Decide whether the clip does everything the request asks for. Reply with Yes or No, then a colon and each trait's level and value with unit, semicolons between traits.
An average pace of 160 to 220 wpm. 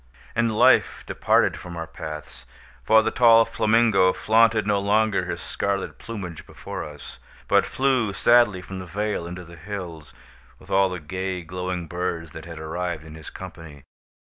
Yes: average, 165 wpm